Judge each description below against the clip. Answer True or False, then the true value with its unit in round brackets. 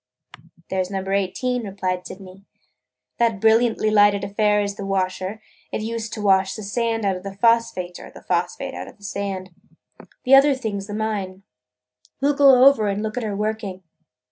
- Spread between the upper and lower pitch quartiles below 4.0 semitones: True (2.6 semitones)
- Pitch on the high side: True (205 Hz)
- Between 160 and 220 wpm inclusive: True (195 wpm)